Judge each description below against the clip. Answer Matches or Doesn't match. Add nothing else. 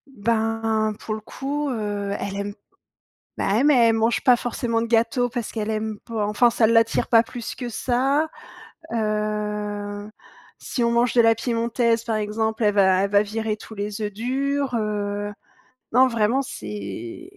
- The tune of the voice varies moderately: Doesn't match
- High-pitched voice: Matches